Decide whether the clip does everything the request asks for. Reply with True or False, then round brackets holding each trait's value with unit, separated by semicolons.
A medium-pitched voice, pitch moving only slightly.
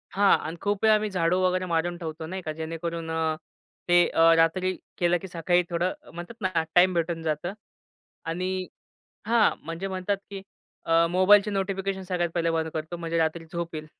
True (175 Hz; 2.2 semitones)